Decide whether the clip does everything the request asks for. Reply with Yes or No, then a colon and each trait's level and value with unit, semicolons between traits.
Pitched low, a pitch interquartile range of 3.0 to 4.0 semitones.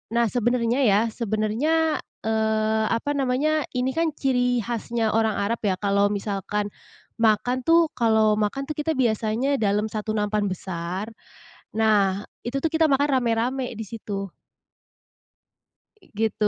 No: high, 225 Hz; average, 3.5 semitones